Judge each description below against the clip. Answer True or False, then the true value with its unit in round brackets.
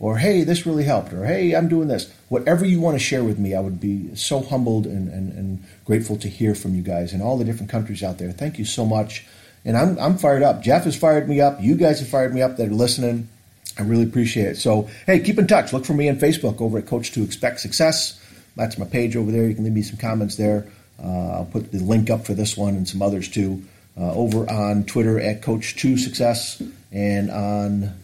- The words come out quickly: True (240 wpm)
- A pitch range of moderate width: True (4.2 semitones)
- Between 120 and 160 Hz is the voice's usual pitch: False (110 Hz)